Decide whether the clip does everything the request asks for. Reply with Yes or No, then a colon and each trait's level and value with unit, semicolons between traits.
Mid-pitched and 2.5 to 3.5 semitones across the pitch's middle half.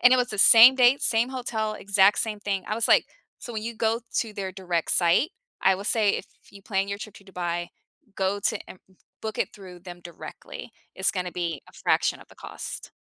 No: high, 200 Hz; average, 3.2 semitones